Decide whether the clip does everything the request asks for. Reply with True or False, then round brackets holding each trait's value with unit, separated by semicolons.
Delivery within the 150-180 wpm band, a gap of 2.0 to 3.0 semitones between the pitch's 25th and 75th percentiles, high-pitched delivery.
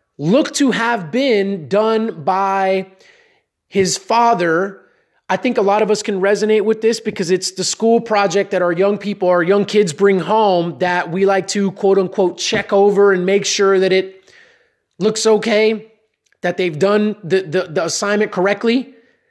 True (170 wpm; 2.6 semitones; 200 Hz)